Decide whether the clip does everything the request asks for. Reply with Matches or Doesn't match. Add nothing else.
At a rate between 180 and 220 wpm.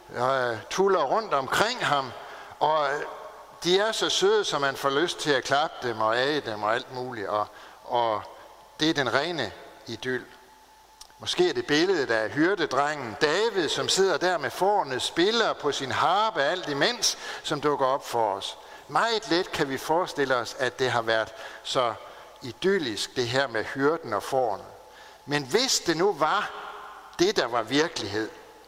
Doesn't match